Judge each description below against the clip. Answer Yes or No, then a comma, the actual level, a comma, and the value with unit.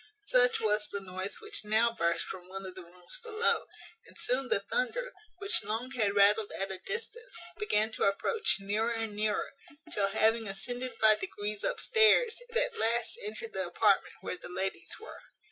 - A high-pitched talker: Yes, high, 225 Hz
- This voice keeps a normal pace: Yes, average, 180 wpm